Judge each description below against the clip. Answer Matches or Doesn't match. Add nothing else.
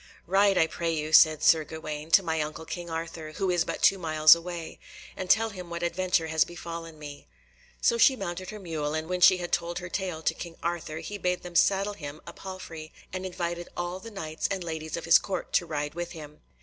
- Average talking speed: Doesn't match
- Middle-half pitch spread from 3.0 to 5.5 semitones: Doesn't match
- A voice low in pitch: Doesn't match